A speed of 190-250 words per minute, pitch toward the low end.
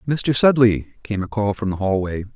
Yes: fast, 205 wpm; low, 105 Hz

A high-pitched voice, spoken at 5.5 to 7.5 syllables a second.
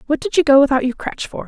Yes: very high, 275 Hz; 6.9 syllables/s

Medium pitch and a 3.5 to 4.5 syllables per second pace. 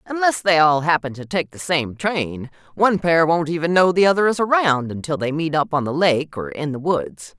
No: medium, 160 Hz; 5.1 syllables/s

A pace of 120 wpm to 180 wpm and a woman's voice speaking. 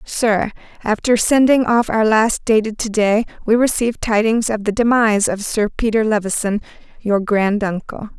Yes: average, 155 wpm; female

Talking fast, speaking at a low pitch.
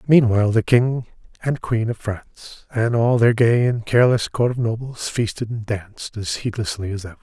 No: average, 190 wpm; low, 115 Hz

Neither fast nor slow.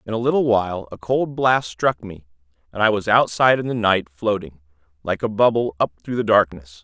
No: fast, 210 wpm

